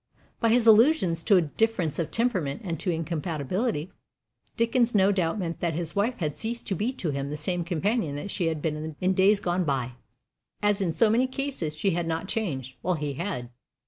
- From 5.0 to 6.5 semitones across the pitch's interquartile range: Yes, wide, 5.5 semitones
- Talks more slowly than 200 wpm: No, fast, 205 wpm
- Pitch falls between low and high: Yes, medium, 175 Hz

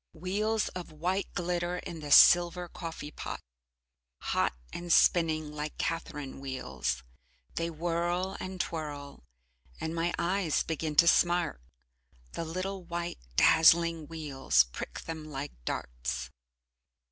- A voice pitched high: No, medium, 165 Hz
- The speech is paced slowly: Yes, slow, 120 wpm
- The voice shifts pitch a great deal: No, average, 2.7 semitones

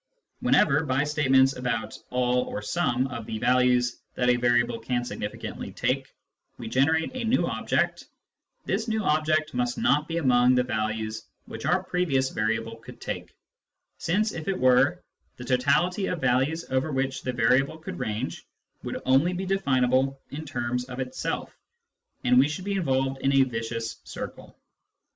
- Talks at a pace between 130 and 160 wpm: No, average, 170 wpm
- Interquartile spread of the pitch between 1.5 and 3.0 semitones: No, average, 4.3 semitones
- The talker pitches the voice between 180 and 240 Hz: No, low, 130 Hz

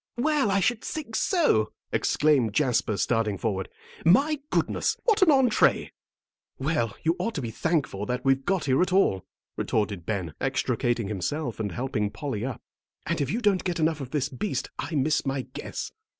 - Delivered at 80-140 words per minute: No, average, 175 wpm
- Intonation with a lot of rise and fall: Yes, wide, 9.0 semitones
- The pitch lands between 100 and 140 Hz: Yes, low, 135 Hz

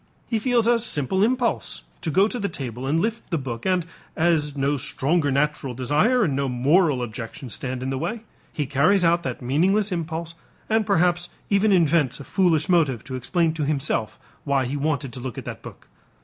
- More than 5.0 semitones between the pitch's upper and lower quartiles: Yes, wide, 5.4 semitones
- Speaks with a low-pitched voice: No, medium, 155 Hz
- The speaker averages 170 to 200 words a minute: Yes, average, 195 wpm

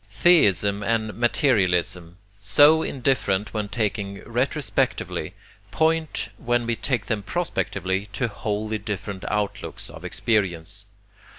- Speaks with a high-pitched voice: No, low, 105 Hz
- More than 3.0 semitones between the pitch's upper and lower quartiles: Yes, average, 3.4 semitones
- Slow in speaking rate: Yes, slow, 105 wpm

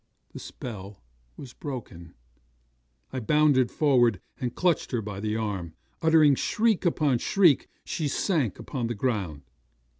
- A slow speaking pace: Yes, slow, 130 wpm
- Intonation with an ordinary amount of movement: No, wide, 6.4 semitones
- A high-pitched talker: No, low, 125 Hz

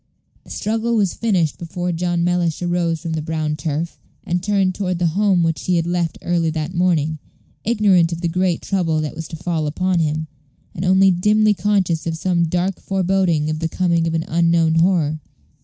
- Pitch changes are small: Yes, narrow, 2.3 semitones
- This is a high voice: No, medium, 170 Hz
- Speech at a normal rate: Yes, average, 190 wpm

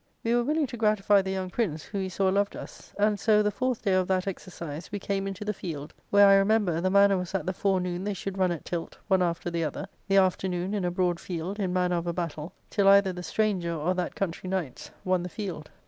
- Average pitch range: No, narrow, 2.2 semitones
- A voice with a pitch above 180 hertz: Yes, high, 190 Hz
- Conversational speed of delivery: No, fast, 250 wpm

